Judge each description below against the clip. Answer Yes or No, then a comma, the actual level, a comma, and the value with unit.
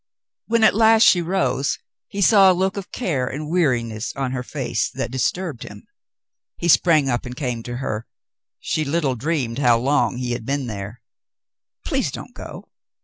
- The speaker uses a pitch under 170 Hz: Yes, medium, 140 Hz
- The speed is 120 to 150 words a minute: No, average, 180 wpm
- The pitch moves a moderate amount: No, wide, 6.3 semitones